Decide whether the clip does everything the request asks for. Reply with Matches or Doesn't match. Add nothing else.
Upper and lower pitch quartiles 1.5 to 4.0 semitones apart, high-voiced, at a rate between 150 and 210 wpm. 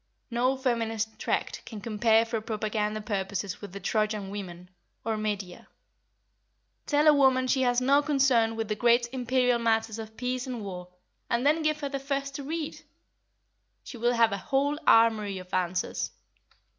Matches